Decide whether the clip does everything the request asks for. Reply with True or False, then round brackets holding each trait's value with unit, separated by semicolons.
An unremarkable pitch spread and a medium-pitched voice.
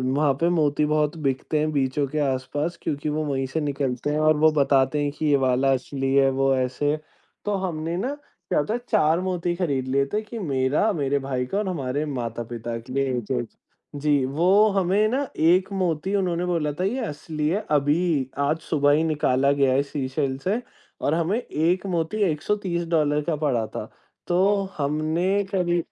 True (4.0 semitones; 150 Hz)